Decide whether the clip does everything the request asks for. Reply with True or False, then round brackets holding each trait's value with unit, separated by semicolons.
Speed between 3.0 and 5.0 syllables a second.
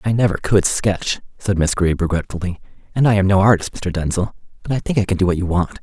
False (6.1 syllables/s)